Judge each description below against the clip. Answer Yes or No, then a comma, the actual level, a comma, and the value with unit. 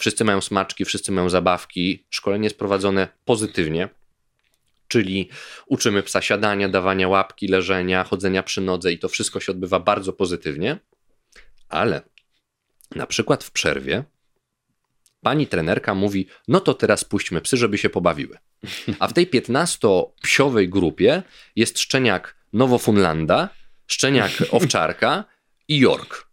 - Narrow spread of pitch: Yes, narrow, 2.2 semitones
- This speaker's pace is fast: No, average, 125 wpm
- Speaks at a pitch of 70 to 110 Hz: Yes, low, 100 Hz